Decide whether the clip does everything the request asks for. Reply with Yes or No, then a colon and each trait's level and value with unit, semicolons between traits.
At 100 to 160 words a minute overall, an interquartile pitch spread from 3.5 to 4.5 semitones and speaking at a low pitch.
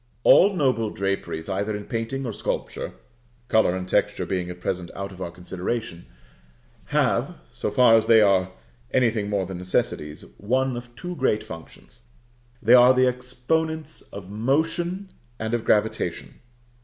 No: average, 150 wpm; average, 5.2 semitones; low, 110 Hz